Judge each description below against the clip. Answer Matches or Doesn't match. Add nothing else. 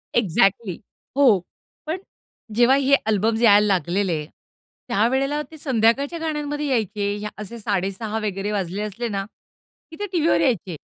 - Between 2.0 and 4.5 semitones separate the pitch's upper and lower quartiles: Doesn't match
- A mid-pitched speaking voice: Doesn't match